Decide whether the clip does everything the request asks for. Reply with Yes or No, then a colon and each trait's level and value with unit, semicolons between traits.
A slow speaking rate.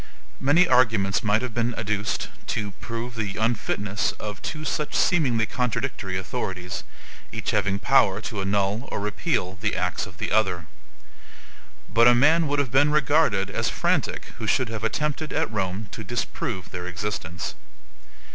No: average, 155 wpm